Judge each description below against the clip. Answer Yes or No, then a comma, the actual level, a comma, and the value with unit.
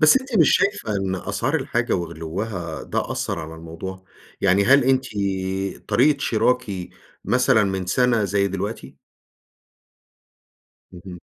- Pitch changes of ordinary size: No, wide, 6.0 semitones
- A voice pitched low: Yes, low, 100 Hz